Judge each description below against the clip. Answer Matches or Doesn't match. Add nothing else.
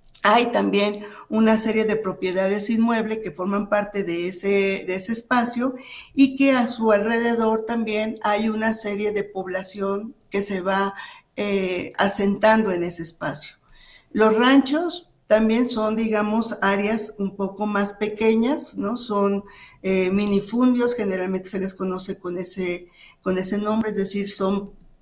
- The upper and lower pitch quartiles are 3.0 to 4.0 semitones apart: Doesn't match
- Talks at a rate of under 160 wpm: Matches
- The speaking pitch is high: Matches